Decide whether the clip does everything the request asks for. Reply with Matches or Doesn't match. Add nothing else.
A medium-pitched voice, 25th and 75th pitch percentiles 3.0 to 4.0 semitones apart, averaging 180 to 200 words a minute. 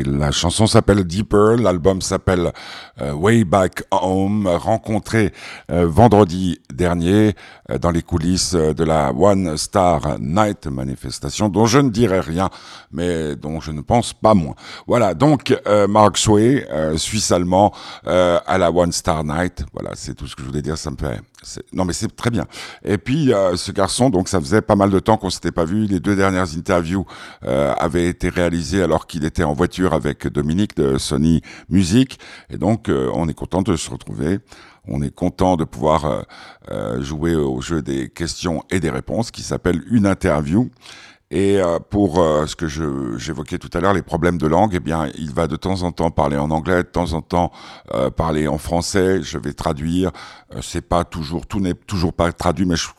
Doesn't match